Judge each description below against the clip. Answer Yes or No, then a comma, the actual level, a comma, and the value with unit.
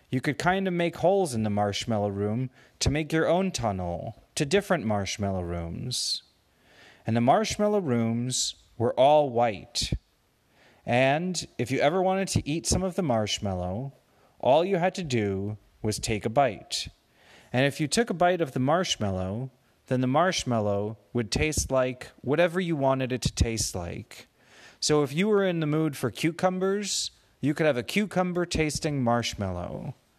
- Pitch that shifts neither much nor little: No, wide, 7.2 semitones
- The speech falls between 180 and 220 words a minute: No, average, 165 wpm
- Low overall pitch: Yes, low, 130 Hz